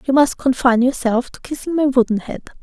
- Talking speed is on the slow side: No, fast, 205 wpm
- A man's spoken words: No, female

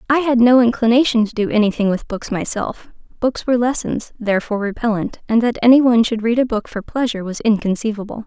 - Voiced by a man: No, female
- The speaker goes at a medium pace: Yes, average, 195 wpm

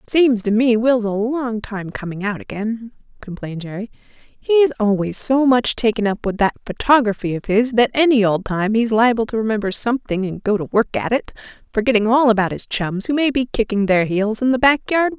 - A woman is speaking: Yes, female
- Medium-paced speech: No, fast, 220 wpm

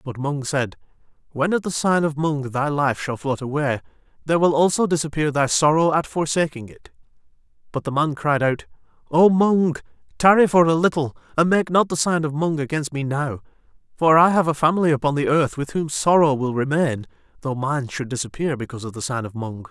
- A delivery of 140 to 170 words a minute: No, fast, 205 wpm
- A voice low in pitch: No, medium, 150 Hz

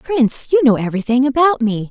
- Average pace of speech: Yes, average, 190 wpm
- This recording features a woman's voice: Yes, female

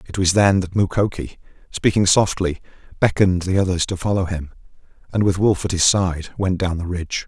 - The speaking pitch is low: Yes, very low, 95 Hz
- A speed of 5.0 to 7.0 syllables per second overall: Yes, 5.6 syllables/s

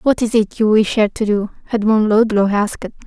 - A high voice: Yes, high, 215 Hz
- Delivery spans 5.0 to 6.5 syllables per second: Yes, 5.2 syllables/s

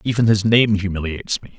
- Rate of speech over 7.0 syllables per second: No, 6.3 syllables/s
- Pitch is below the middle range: Yes, low, 105 Hz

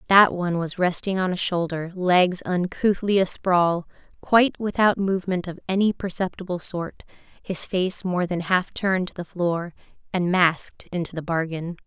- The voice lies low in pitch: No, medium, 180 Hz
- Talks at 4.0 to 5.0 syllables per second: Yes, 4.8 syllables/s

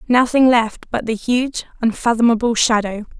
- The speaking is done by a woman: Yes, female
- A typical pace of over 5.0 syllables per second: No, 4.8 syllables/s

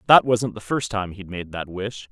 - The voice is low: Yes, low, 105 Hz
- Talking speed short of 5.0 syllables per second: Yes, 4.7 syllables/s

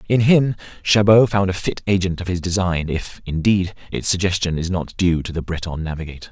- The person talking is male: Yes, male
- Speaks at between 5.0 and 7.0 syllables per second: Yes, 5.5 syllables/s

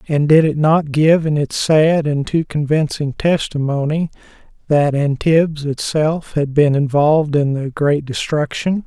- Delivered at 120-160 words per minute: Yes, average, 150 wpm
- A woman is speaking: No, male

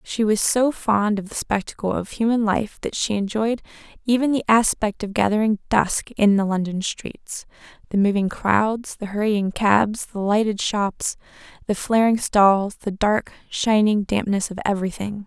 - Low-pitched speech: No, high, 210 Hz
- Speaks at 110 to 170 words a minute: Yes, average, 155 wpm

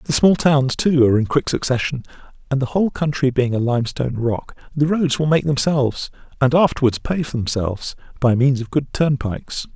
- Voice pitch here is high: No, low, 135 Hz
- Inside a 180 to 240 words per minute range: Yes, average, 185 wpm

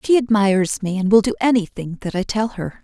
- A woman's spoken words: Yes, female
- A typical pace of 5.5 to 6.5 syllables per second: Yes, 5.7 syllables/s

